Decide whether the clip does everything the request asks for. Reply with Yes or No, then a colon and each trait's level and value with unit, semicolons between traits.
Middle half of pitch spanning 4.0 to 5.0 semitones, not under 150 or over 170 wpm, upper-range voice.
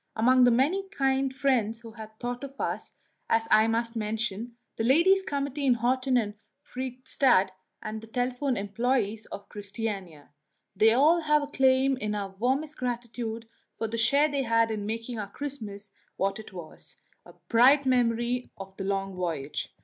No: average, 3.6 semitones; average, 165 wpm; high, 235 Hz